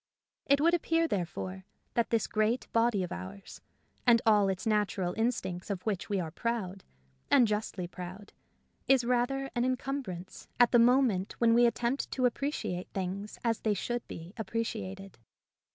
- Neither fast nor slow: Yes, average, 155 wpm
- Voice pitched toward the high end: Yes, high, 220 Hz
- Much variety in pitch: No, average, 4.3 semitones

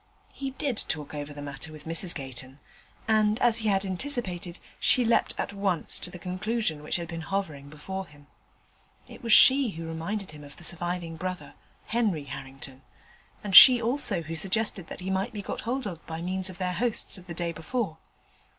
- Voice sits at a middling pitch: Yes, medium, 180 Hz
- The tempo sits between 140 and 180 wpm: No, average, 195 wpm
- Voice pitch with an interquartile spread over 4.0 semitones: Yes, average, 4.8 semitones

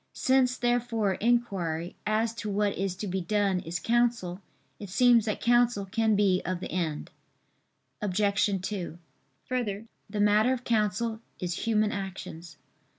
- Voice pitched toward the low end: No, high, 210 Hz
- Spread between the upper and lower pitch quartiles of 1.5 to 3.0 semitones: No, average, 3.5 semitones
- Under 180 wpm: Yes, average, 145 wpm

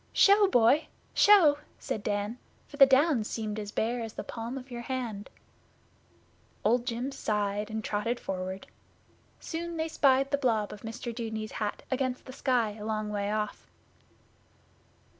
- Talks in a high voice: Yes, high, 230 Hz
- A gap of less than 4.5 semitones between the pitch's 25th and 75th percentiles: Yes, average, 4.0 semitones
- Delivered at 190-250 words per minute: No, average, 155 wpm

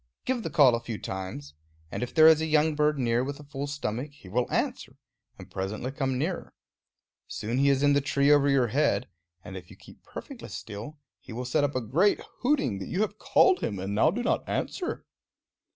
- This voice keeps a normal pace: No, fast, 215 wpm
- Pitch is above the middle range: No, medium, 140 Hz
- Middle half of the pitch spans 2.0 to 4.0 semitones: No, average, 4.7 semitones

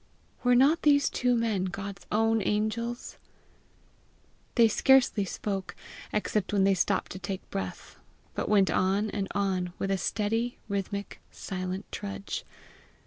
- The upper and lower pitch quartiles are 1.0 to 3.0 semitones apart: Yes, average, 2.7 semitones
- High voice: Yes, high, 205 Hz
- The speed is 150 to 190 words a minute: No, slow, 135 wpm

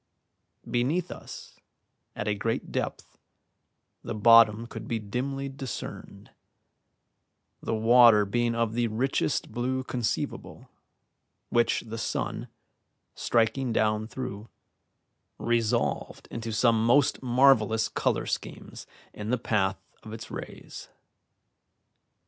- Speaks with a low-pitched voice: Yes, low, 115 Hz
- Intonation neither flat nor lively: No, narrow, 2.2 semitones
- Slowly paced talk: Yes, slow, 105 wpm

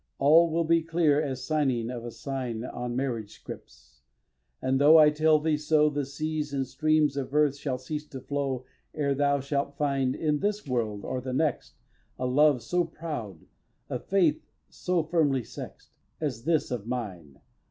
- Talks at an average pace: Yes, average, 175 wpm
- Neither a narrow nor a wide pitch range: Yes, average, 3.4 semitones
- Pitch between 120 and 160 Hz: Yes, medium, 140 Hz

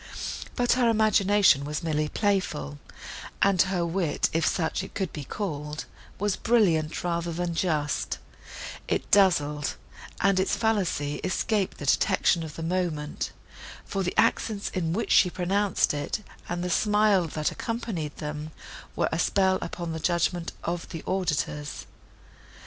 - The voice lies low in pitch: No, medium, 175 Hz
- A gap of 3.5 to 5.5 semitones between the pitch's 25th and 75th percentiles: Yes, average, 4.2 semitones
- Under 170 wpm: Yes, average, 145 wpm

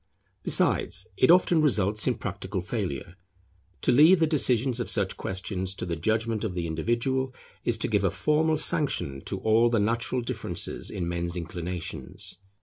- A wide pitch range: Yes, wide, 5.7 semitones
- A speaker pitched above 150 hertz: No, low, 110 Hz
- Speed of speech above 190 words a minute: No, average, 160 wpm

